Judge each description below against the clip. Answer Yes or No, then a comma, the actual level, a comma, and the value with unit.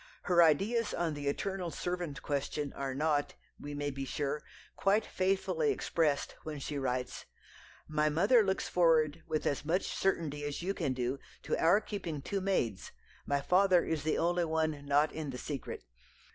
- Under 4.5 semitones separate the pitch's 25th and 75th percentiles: Yes, average, 4.0 semitones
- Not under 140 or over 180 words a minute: Yes, average, 170 wpm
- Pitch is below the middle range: No, medium, 155 Hz